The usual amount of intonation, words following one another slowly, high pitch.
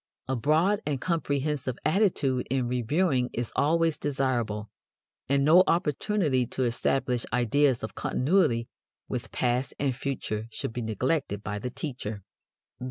No: average, 3.9 semitones; slow, 130 wpm; low, 130 Hz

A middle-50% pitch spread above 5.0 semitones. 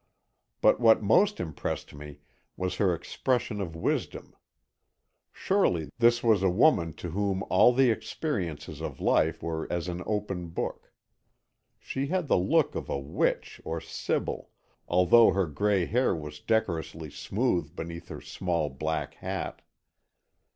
Yes: wide, 5.5 semitones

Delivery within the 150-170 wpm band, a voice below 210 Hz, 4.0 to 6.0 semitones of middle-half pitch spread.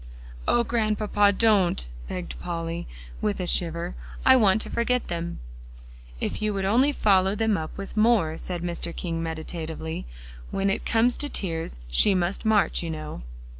Yes: average, 160 wpm; high, 190 Hz; average, 4.4 semitones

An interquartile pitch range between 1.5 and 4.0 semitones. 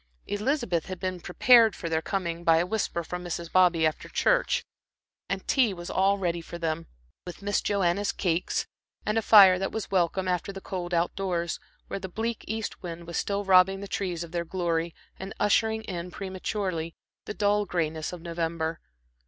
Yes: average, 2.9 semitones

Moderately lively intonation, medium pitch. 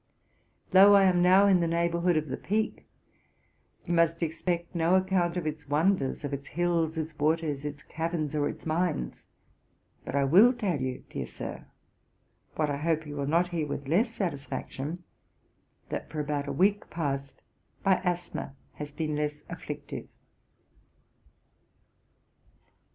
Yes: average, 3.3 semitones; medium, 165 Hz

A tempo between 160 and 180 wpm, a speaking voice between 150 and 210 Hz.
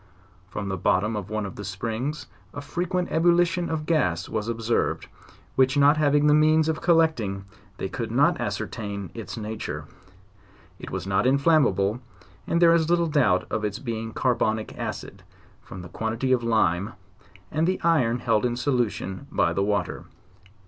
No: average, 170 wpm; low, 120 Hz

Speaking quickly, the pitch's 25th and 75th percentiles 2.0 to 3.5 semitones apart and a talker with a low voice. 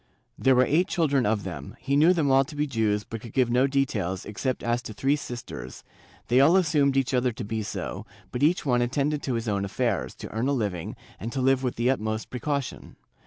No: fast, 225 wpm; average, 4.0 semitones; low, 125 Hz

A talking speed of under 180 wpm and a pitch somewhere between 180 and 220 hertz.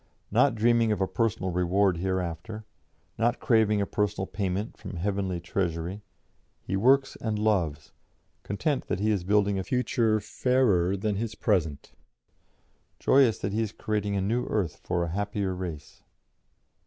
No: average, 150 wpm; low, 100 Hz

